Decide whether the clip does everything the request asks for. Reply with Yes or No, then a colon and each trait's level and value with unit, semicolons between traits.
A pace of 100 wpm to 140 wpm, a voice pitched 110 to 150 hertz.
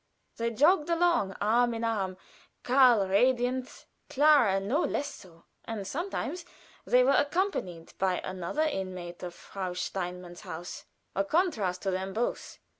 No: slow, 135 wpm; high, 215 Hz